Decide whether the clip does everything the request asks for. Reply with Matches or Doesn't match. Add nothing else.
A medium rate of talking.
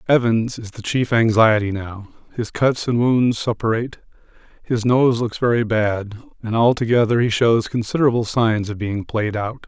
Matches